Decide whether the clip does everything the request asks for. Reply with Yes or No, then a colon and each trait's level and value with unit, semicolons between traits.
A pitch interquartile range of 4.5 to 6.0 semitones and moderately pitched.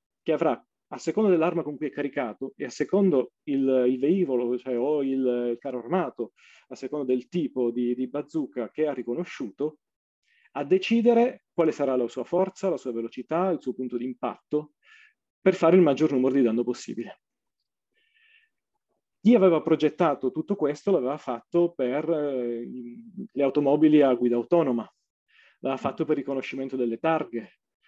Yes: wide, 5.4 semitones; medium, 145 Hz